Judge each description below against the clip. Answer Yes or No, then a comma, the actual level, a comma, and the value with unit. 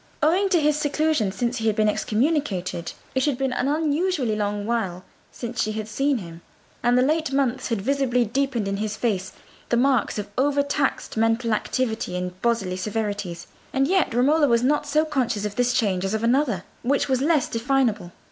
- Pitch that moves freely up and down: No, average, 4.8 semitones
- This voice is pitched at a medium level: No, high, 240 Hz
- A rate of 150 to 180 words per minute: No, average, 190 wpm